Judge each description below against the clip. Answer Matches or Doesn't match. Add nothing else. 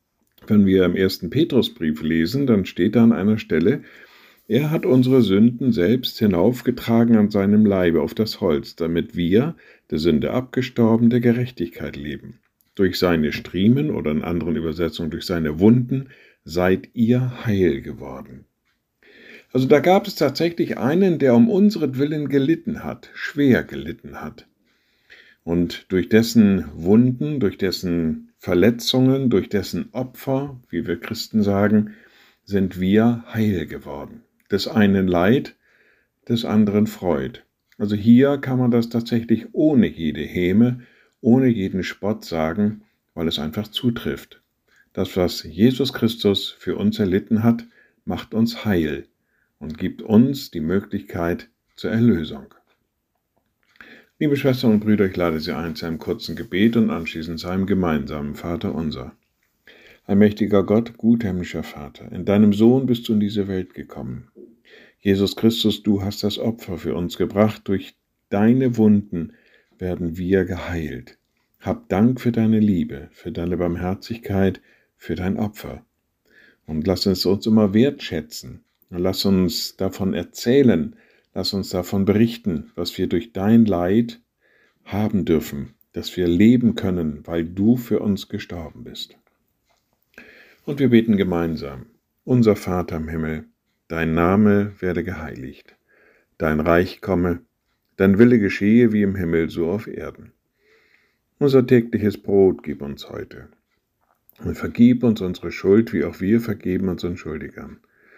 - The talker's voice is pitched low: Matches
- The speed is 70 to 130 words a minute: Doesn't match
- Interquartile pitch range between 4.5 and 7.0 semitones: Matches